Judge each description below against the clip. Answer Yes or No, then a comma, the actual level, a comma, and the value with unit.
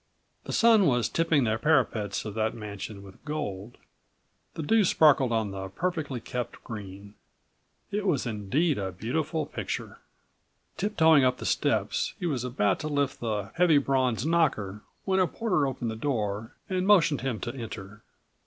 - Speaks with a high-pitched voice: No, low, 125 Hz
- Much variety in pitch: Yes, wide, 7.0 semitones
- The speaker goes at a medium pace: Yes, average, 160 wpm